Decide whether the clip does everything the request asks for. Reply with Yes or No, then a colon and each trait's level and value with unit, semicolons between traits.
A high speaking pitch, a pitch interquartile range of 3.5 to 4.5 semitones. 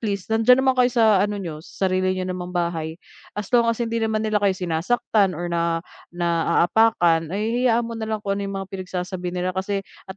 Yes: high, 195 Hz; average, 3.9 semitones